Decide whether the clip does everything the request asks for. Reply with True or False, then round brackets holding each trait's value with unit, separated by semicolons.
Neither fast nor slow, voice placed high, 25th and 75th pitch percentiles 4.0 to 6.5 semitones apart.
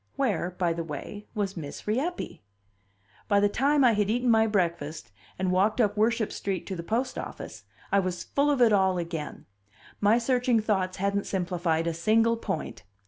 True (180 wpm; 200 Hz; 4.3 semitones)